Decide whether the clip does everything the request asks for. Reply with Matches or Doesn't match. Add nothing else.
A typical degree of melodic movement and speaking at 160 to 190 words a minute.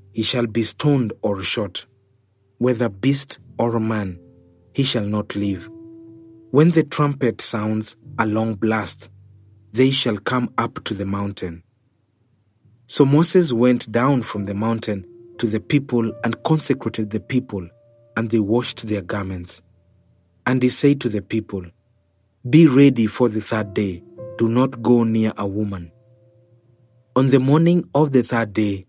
Doesn't match